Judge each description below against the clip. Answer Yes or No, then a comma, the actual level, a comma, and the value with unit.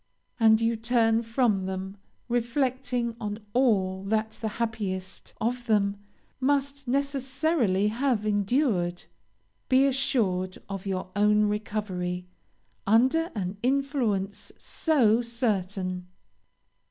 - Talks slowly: Yes, slow, 100 wpm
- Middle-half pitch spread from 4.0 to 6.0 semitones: Yes, average, 4.4 semitones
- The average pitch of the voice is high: Yes, high, 220 Hz